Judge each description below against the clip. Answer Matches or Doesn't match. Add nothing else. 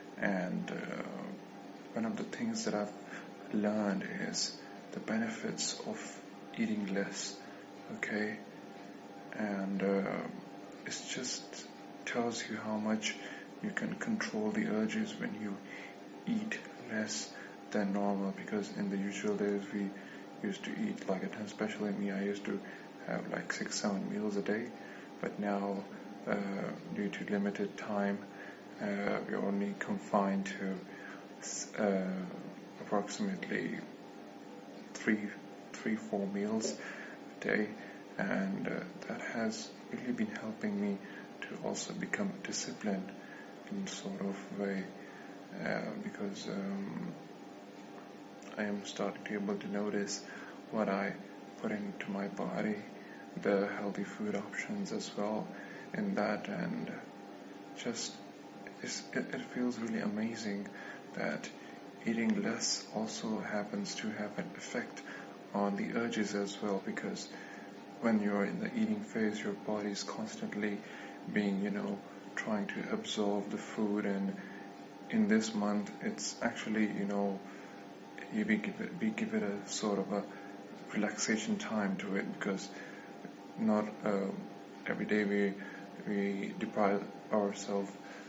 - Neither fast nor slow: Doesn't match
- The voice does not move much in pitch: Matches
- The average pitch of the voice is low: Matches